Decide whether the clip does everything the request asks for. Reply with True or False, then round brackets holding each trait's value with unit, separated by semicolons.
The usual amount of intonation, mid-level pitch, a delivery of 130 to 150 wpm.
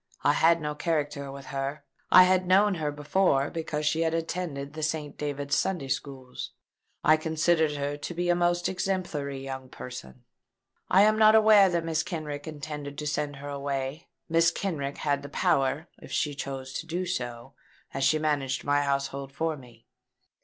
False (3.2 semitones; 150 Hz; 175 wpm)